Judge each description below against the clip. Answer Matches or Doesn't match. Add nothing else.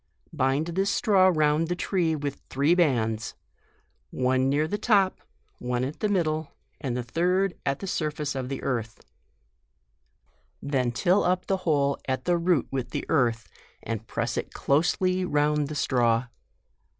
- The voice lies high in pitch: Doesn't match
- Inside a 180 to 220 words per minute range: Doesn't match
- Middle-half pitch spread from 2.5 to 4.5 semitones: Doesn't match